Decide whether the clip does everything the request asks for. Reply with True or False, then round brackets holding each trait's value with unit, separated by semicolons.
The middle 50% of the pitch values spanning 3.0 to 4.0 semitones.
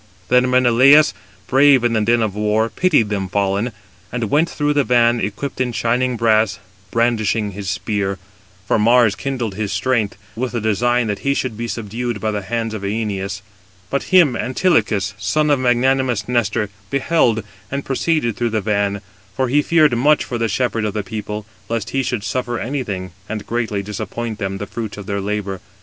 True (3.4 semitones)